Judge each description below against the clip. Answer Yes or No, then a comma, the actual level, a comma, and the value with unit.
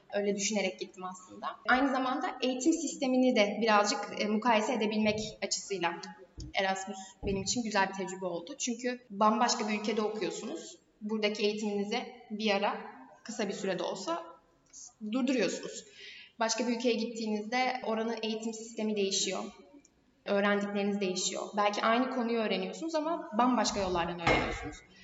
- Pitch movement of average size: Yes, average, 3.4 semitones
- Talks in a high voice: Yes, high, 215 Hz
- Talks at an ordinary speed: Yes, average, 125 wpm